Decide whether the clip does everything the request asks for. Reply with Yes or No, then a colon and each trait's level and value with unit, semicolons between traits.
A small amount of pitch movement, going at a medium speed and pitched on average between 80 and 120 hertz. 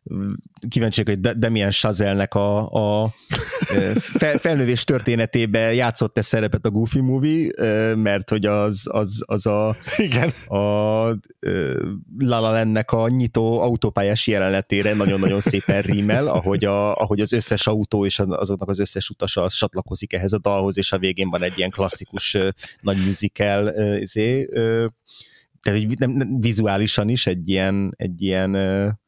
Yes: narrow, 2.3 semitones; average, 130 wpm; low, 105 Hz